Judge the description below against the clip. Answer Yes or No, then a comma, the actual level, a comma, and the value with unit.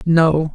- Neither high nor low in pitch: Yes, medium, 160 Hz